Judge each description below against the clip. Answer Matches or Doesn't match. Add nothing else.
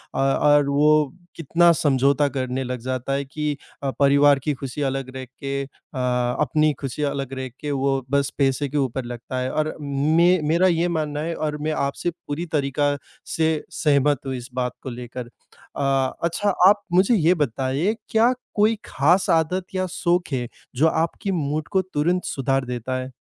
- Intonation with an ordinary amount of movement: Matches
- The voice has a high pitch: Doesn't match